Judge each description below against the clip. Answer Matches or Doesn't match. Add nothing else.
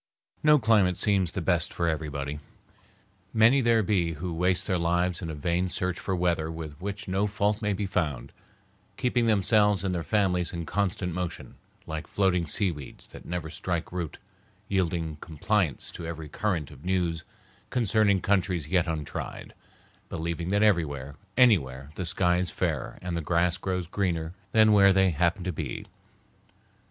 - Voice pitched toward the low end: Matches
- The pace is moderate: Matches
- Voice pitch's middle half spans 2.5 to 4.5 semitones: Matches